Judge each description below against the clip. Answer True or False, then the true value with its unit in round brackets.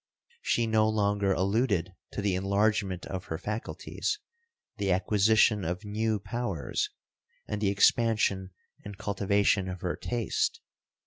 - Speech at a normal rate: False (125 wpm)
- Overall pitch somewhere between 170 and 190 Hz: False (100 Hz)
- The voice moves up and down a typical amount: False (2.2 semitones)